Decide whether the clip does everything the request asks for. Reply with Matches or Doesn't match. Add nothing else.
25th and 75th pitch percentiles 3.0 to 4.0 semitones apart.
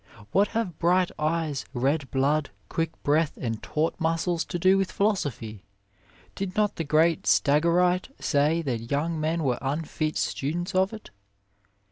Matches